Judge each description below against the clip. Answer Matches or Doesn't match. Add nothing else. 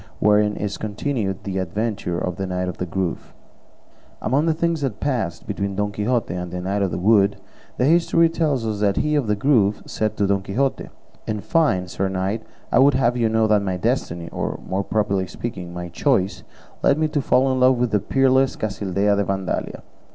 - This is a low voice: Matches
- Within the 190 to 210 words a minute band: Matches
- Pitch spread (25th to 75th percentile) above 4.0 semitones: Matches